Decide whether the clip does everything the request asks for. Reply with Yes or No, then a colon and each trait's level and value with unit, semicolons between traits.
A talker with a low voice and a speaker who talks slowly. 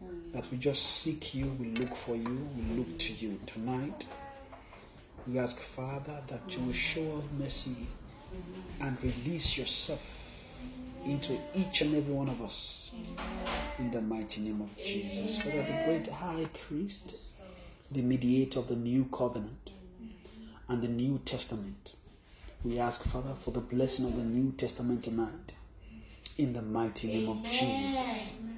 No: low, 125 Hz; average, 150 wpm